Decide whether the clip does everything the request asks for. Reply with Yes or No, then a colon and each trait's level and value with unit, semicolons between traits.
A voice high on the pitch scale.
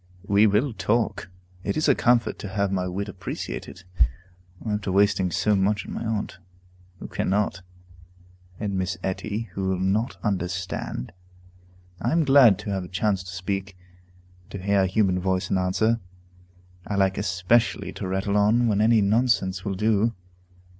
No: low, 100 Hz